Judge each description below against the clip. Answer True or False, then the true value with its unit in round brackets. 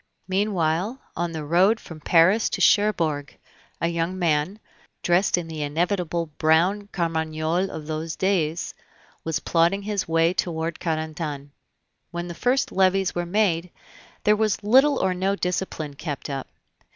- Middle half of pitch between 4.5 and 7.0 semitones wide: False (3.3 semitones)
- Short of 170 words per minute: True (140 wpm)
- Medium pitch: True (170 Hz)